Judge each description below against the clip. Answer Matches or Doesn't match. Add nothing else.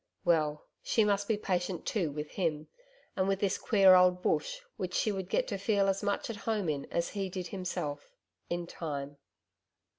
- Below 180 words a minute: Doesn't match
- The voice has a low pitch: Doesn't match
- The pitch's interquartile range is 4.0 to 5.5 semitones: Doesn't match